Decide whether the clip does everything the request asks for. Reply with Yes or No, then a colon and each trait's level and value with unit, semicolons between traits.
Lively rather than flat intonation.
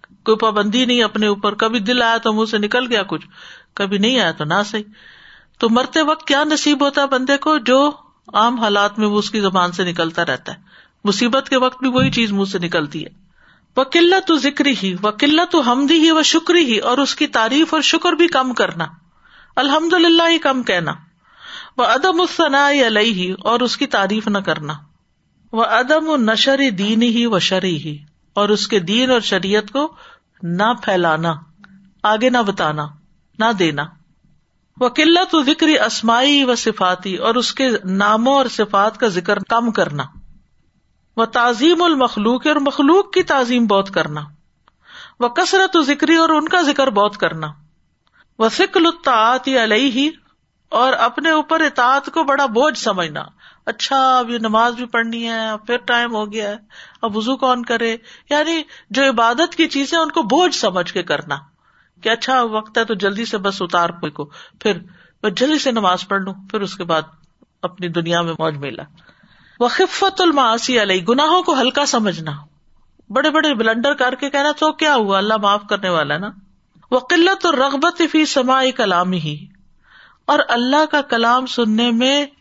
Yes: wide, 6.1 semitones